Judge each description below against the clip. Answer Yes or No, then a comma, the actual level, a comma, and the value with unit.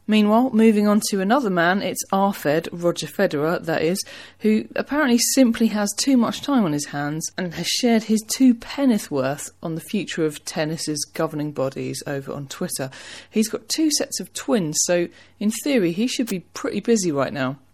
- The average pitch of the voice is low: No, high, 195 Hz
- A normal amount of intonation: No, wide, 6.4 semitones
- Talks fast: No, average, 185 wpm